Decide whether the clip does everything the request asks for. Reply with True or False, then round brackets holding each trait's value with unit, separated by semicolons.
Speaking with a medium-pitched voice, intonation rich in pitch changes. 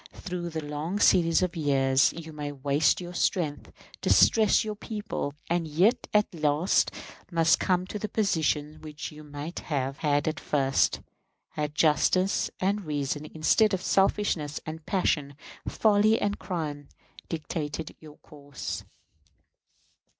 False (160 Hz; 3.9 semitones)